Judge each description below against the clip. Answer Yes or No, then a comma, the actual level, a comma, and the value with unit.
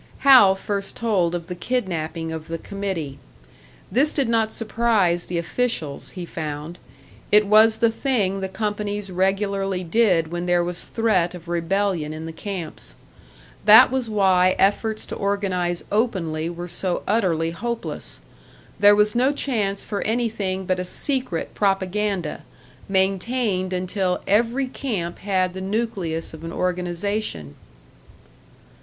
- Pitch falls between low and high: No, high, 195 Hz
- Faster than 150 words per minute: No, slow, 135 wpm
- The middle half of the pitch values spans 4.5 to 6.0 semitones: No, average, 3.7 semitones